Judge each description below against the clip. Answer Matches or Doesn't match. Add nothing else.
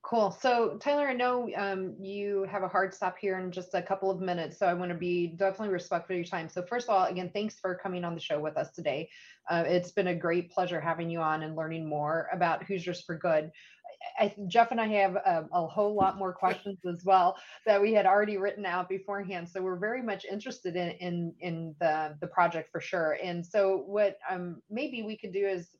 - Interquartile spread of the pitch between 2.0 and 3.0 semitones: Matches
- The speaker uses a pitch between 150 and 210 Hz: Matches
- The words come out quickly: Matches